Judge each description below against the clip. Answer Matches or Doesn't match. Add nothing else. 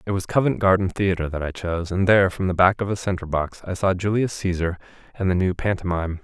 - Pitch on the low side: Matches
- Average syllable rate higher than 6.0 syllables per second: Matches